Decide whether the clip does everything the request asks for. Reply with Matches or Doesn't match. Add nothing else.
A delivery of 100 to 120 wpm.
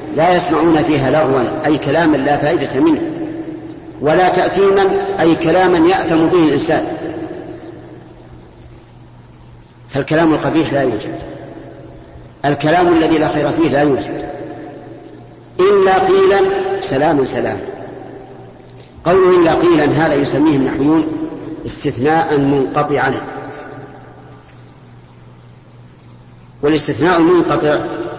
Doesn't match